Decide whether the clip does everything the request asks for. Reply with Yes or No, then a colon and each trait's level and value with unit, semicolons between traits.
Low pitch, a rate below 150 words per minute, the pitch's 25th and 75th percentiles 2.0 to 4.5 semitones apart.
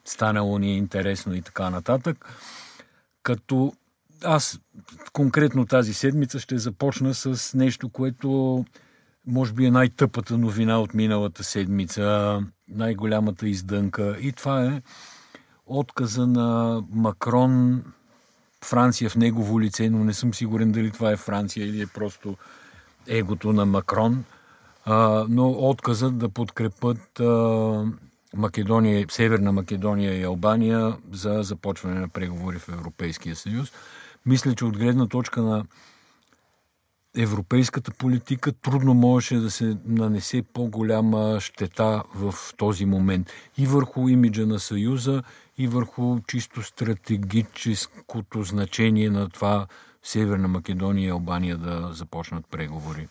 Yes: low, 110 Hz; average, 120 wpm; average, 3.4 semitones